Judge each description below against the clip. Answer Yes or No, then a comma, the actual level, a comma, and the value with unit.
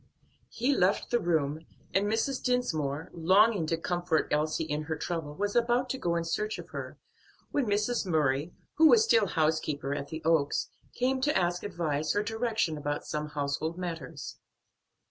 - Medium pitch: Yes, medium, 170 Hz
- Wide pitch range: Yes, wide, 6.2 semitones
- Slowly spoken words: No, average, 165 wpm